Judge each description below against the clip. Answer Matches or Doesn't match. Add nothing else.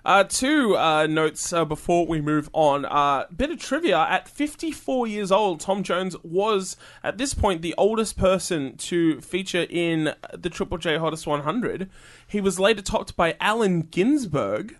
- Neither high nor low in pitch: Matches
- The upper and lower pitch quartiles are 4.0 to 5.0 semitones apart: Matches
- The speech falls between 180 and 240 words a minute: Doesn't match